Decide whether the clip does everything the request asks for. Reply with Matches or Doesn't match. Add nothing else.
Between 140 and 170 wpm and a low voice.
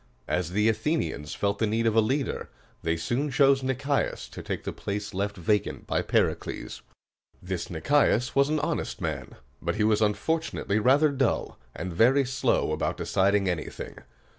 Matches